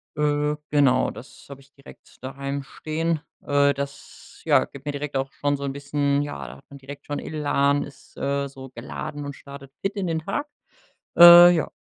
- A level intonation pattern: Yes, narrow, 1.3 semitones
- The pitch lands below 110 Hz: No, medium, 140 Hz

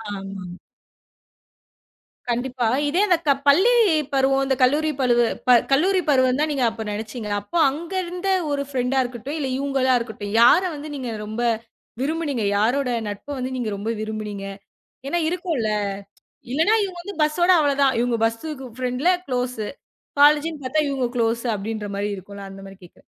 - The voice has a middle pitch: No, very high, 255 Hz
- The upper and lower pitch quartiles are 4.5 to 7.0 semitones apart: Yes, average, 4.9 semitones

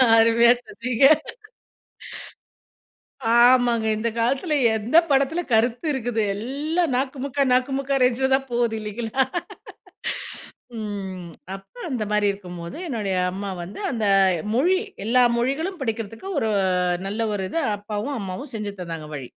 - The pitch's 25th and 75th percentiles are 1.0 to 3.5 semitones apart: No, average, 4.3 semitones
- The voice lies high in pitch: Yes, high, 235 Hz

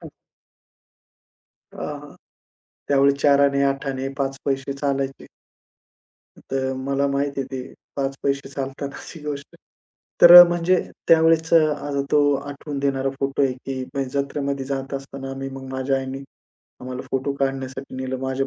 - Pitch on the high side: No, medium, 140 Hz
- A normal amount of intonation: No, narrow, 1.0 semitones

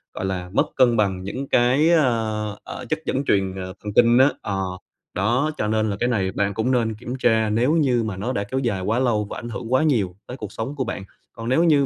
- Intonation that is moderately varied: Yes, average, 4.2 semitones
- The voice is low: Yes, low, 115 Hz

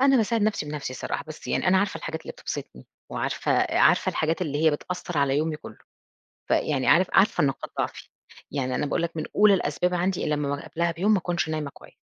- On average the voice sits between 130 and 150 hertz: No, medium, 160 Hz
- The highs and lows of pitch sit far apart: No, average, 3.9 semitones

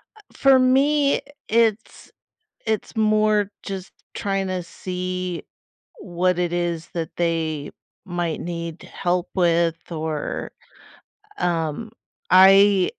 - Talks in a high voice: No, medium, 180 Hz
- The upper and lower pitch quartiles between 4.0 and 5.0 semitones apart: No, average, 3.6 semitones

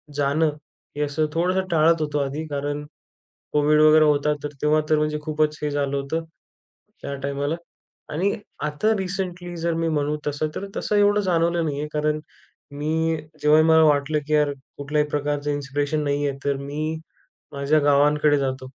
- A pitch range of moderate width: No, narrow, 1.8 semitones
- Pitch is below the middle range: No, medium, 150 Hz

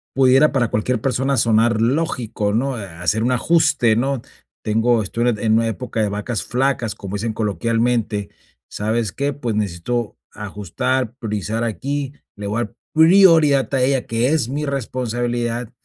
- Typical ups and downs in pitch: Yes, average, 3.5 semitones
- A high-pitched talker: No, low, 120 Hz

